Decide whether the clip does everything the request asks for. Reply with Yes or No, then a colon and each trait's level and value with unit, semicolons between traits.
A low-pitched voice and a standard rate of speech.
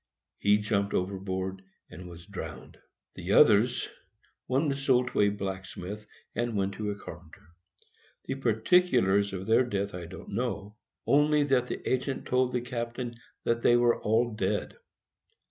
Yes: low, 110 Hz; average, 145 wpm